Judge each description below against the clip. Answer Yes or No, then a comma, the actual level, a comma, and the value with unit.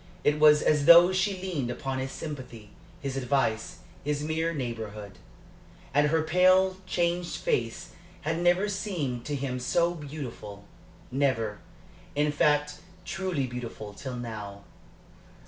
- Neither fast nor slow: No, slow, 130 wpm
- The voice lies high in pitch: No, medium, 145 Hz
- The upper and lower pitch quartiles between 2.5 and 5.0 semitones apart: No, wide, 5.5 semitones